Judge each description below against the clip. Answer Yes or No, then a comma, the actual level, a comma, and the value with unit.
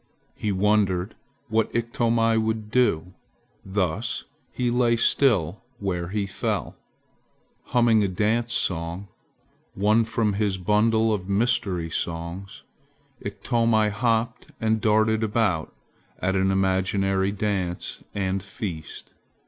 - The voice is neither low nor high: No, low, 105 Hz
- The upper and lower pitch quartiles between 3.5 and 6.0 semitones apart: No, average, 3.0 semitones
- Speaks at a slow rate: Yes, slow, 110 wpm